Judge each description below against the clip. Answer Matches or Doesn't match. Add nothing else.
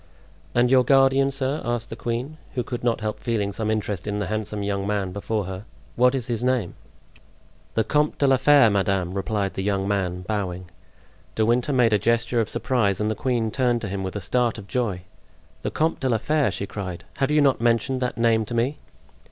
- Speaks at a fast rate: Matches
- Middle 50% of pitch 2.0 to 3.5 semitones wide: Doesn't match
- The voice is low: Matches